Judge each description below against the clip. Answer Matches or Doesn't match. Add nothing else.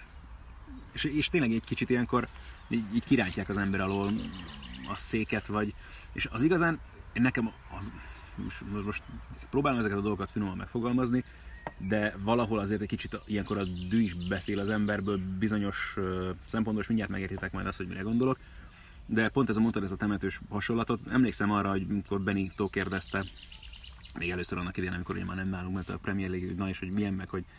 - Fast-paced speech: Matches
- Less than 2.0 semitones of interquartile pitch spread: Doesn't match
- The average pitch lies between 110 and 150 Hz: Doesn't match